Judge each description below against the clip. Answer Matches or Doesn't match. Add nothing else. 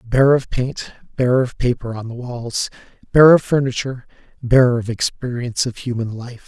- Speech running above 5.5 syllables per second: Doesn't match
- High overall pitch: Doesn't match